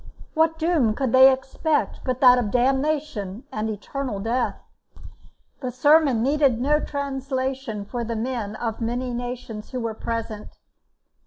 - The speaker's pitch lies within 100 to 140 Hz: No, very high, 255 Hz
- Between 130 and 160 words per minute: Yes, average, 140 wpm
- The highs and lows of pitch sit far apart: No, average, 3.4 semitones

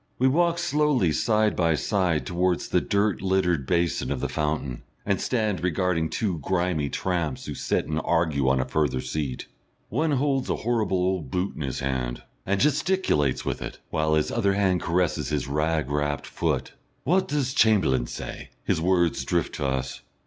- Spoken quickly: No, average, 175 wpm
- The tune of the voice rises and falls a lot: Yes, wide, 6.0 semitones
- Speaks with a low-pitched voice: Yes, very low, 90 Hz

